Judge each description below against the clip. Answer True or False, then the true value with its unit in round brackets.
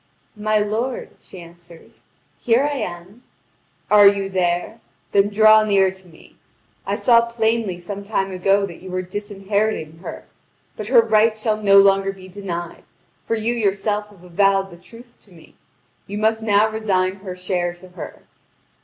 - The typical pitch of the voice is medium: False (200 Hz)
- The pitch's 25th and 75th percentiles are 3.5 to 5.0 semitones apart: False (2.8 semitones)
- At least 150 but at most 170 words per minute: True (160 wpm)